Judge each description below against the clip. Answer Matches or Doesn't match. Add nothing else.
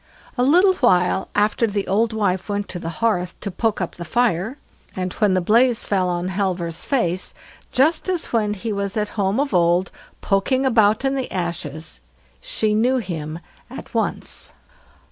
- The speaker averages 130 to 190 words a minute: Matches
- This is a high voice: Matches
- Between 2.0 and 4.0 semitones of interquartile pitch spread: Doesn't match